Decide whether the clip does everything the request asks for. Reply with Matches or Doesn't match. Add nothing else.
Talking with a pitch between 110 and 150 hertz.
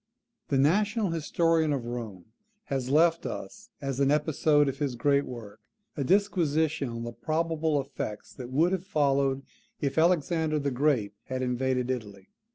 Matches